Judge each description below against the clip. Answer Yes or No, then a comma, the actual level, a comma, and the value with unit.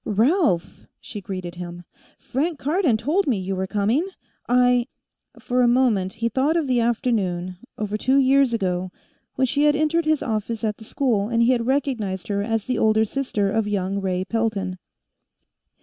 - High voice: Yes, high, 225 Hz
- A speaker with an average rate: Yes, average, 180 wpm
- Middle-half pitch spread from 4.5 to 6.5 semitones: Yes, average, 4.9 semitones